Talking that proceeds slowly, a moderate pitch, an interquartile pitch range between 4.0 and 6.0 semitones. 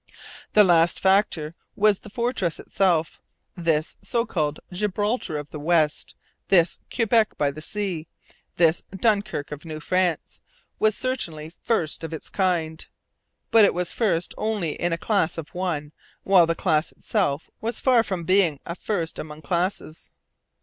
No: average, 150 wpm; medium, 175 Hz; average, 4.6 semitones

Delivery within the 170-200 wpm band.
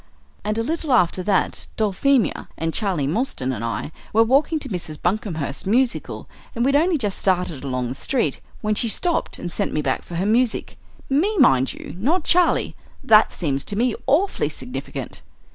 Yes: average, 180 wpm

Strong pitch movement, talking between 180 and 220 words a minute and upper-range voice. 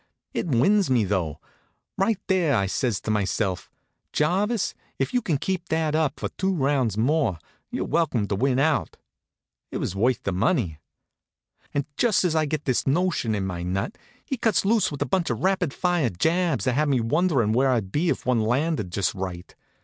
No: wide, 8.2 semitones; average, 190 wpm; medium, 140 Hz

